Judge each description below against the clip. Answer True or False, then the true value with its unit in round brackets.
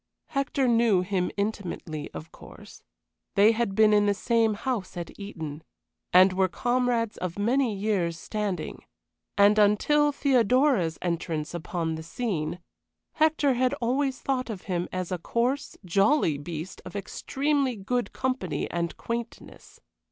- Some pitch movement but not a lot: False (5.7 semitones)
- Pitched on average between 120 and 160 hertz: False (205 Hz)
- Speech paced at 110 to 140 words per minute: True (135 wpm)